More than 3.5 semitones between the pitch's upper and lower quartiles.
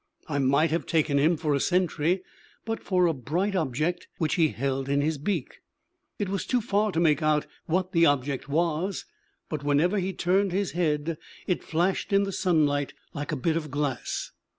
Yes: average, 4.1 semitones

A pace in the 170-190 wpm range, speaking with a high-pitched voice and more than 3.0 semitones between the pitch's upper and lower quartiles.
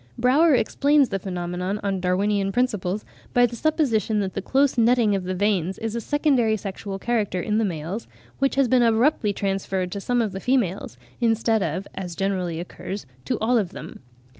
Yes: average, 185 wpm; high, 210 Hz; average, 4.2 semitones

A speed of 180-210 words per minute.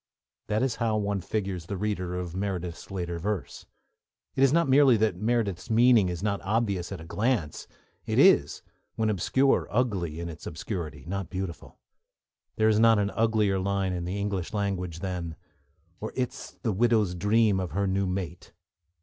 No: average, 170 wpm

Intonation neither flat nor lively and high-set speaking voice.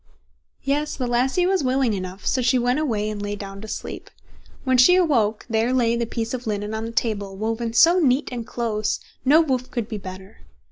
Yes: average, 3.4 semitones; high, 235 Hz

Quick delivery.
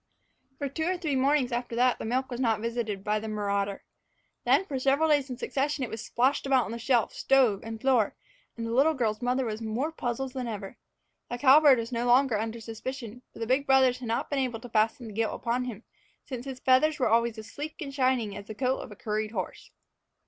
Yes: fast, 230 wpm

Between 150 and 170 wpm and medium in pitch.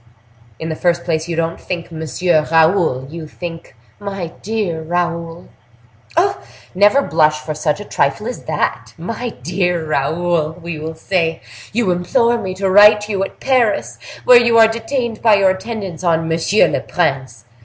Yes: average, 160 wpm; medium, 175 Hz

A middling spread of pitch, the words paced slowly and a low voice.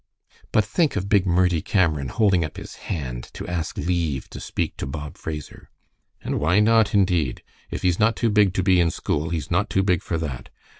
No: average, 4.3 semitones; fast, 205 wpm; very low, 90 Hz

